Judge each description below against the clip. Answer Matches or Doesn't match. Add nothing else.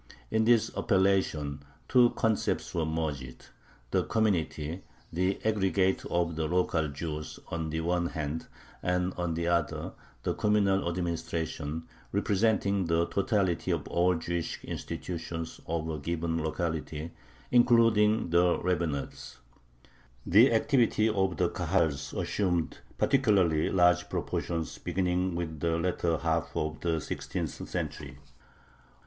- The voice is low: Matches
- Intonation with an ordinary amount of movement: Matches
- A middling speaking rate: Doesn't match